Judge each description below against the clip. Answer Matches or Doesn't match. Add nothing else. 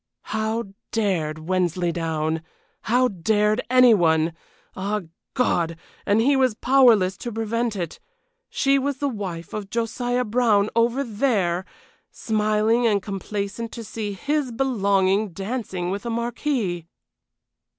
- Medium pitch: Doesn't match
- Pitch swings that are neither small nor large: Matches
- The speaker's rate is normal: Doesn't match